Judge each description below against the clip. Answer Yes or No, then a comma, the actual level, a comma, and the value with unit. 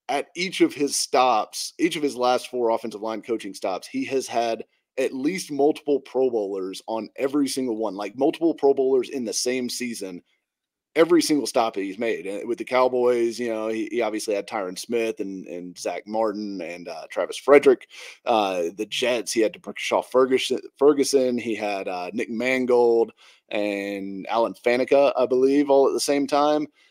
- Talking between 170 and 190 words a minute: Yes, average, 185 wpm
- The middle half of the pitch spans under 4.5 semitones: No, average, 4.8 semitones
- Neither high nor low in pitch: No, low, 125 Hz